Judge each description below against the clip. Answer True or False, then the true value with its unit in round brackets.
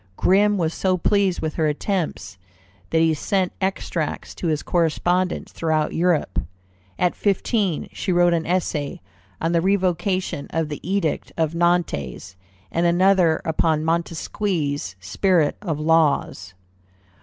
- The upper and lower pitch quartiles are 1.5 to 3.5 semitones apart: True (3.0 semitones)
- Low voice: False (170 Hz)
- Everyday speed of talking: False (130 wpm)